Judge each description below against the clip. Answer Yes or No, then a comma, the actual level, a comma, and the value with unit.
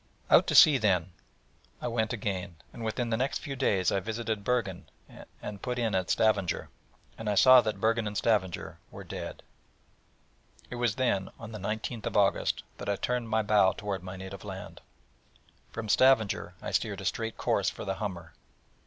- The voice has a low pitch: Yes, low, 105 Hz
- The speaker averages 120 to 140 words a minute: No, average, 180 wpm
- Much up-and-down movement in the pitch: No, average, 3.1 semitones